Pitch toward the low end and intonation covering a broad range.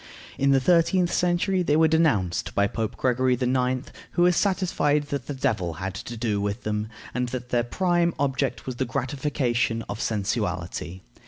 Yes: low, 130 Hz; wide, 5.7 semitones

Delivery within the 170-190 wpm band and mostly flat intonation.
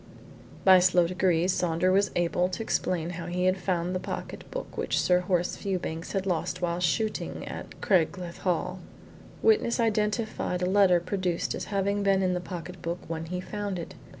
Yes: average, 175 wpm; narrow, 1.9 semitones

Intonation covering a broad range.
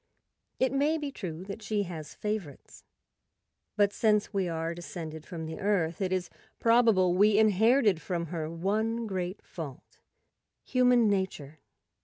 No: average, 4.5 semitones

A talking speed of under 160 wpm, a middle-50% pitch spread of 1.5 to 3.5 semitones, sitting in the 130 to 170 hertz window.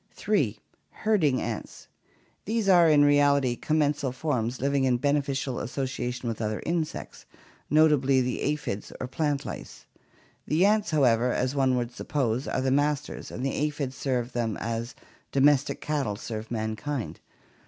Yes: average, 145 wpm; average, 3.2 semitones; low, 135 Hz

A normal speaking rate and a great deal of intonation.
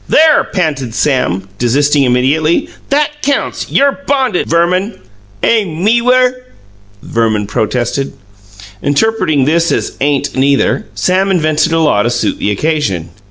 No: slow, 120 wpm; wide, 8.4 semitones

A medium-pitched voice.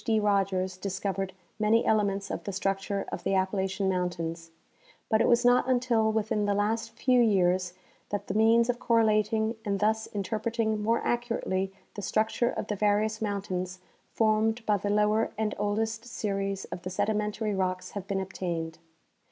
No: high, 210 Hz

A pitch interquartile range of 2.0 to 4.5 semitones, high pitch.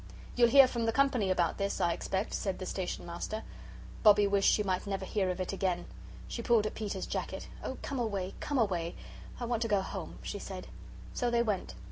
Yes: average, 3.8 semitones; high, 205 Hz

